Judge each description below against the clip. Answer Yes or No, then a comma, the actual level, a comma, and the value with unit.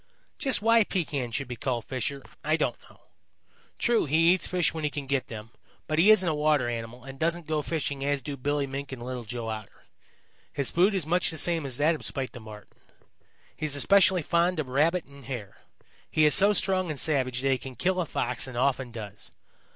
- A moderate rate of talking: No, fast, 220 wpm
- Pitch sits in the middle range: Yes, medium, 145 Hz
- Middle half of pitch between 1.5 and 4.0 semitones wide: No, average, 4.7 semitones